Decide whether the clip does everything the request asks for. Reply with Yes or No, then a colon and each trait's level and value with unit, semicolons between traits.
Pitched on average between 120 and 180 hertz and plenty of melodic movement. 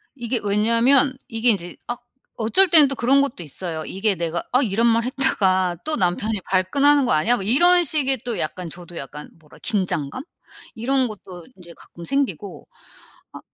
No: high, 220 Hz; wide, 6.6 semitones